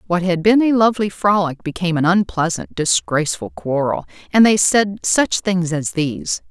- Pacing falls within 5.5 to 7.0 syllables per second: No, 5.0 syllables/s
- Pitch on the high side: No, medium, 170 Hz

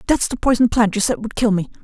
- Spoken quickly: Yes, fast, 295 wpm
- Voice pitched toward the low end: No, high, 225 Hz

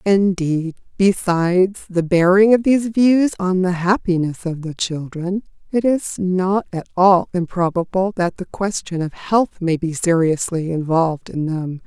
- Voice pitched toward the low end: No, medium, 180 Hz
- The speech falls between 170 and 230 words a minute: No, average, 150 wpm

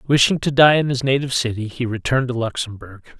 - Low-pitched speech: Yes, low, 125 Hz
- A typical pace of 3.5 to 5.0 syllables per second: No, 6.3 syllables/s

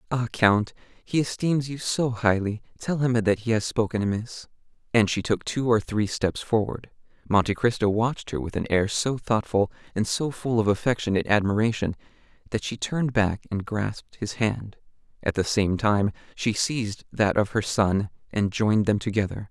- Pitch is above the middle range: No, low, 110 Hz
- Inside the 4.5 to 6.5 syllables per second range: Yes, 5.0 syllables/s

